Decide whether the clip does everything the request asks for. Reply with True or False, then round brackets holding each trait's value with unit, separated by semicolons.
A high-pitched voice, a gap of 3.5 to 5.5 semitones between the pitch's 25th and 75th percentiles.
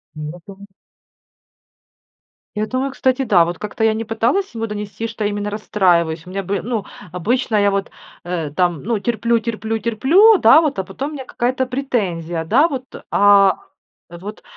True (210 Hz; 4.3 semitones)